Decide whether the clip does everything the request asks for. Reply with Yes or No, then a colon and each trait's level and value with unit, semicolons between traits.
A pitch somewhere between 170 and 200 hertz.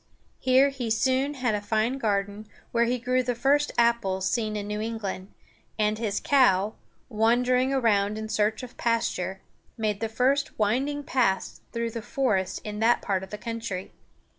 No: high, 225 Hz